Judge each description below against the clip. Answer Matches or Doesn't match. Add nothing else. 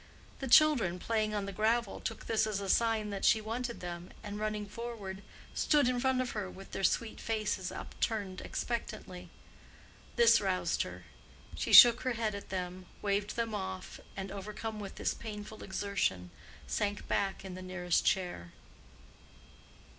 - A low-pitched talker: Doesn't match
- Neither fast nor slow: Matches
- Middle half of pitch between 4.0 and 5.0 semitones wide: Doesn't match